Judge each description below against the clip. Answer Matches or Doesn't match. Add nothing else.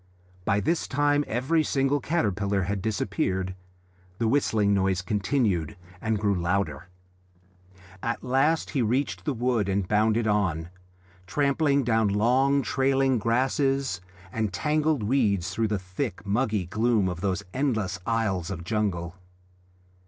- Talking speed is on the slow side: Matches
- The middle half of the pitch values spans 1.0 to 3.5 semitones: Doesn't match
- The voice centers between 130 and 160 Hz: Doesn't match